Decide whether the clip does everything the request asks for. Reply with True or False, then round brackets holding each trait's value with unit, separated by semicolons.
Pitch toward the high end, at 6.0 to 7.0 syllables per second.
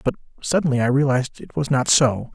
False (135 Hz; 6.2 syllables/s)